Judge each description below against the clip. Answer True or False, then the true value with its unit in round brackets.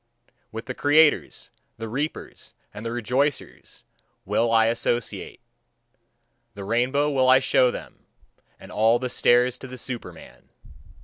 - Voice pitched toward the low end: True (125 Hz)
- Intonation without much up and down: True (2.3 semitones)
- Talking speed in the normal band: False (130 wpm)